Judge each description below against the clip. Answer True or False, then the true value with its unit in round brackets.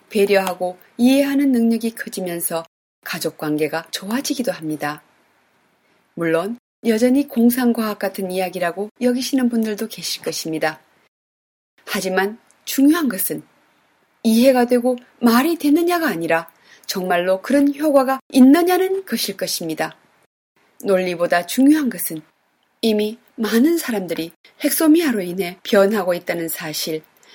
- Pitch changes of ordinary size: False (6.6 semitones)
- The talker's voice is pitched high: True (210 Hz)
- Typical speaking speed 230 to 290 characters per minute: True (285 characters per minute)